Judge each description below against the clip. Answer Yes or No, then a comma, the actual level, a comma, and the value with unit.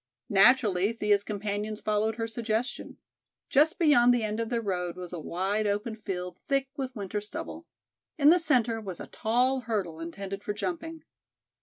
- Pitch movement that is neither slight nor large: Yes, average, 3.8 semitones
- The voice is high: Yes, high, 215 Hz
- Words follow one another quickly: No, average, 165 wpm